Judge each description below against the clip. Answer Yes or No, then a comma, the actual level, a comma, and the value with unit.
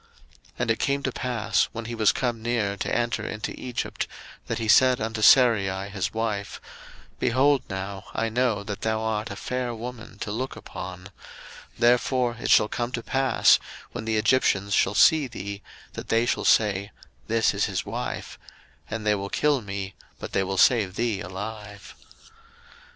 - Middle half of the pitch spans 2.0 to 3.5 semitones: Yes, average, 3.0 semitones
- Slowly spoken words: No, average, 175 wpm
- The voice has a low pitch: Yes, low, 110 Hz